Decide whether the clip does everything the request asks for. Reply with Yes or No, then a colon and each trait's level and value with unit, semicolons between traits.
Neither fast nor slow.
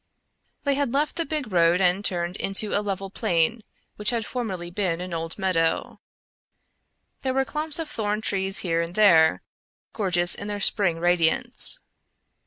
Yes: average, 160 wpm